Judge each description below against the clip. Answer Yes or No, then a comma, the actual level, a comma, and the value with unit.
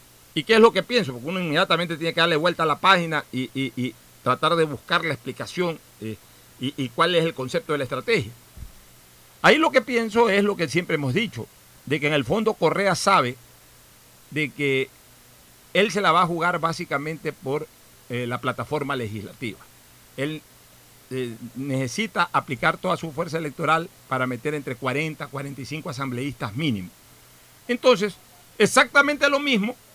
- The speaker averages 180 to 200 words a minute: No, average, 170 wpm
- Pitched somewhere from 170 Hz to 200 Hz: No, medium, 150 Hz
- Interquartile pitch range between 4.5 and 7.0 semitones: Yes, wide, 5.4 semitones